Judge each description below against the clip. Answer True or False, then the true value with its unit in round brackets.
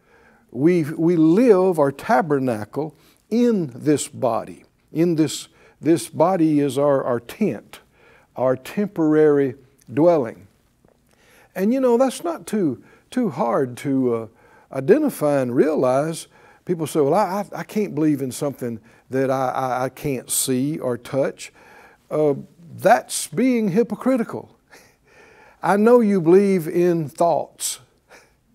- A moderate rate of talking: False (125 wpm)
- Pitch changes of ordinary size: False (6.9 semitones)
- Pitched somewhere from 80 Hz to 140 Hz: False (155 Hz)